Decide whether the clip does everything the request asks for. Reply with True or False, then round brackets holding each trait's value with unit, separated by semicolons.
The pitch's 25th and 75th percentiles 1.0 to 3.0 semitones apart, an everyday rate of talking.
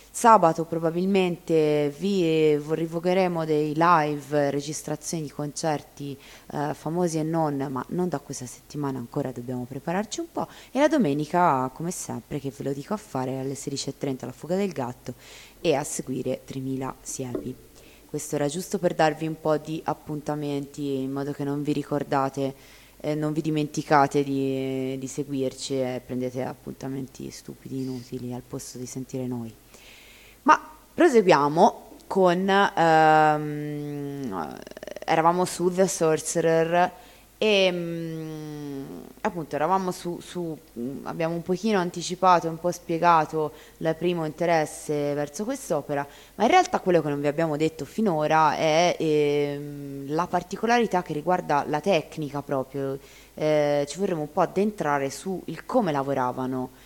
False (4.0 semitones; 140 wpm)